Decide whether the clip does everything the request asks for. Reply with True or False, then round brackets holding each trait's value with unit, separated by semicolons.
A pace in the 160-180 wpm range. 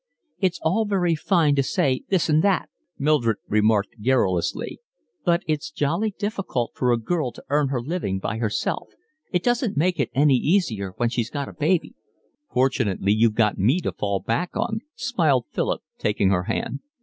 True (175 wpm)